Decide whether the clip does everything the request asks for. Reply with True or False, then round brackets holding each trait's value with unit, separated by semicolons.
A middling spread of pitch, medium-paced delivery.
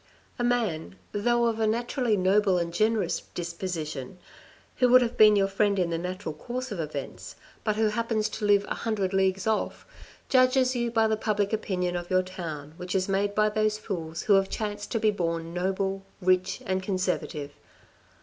True (3.2 semitones; 185 wpm)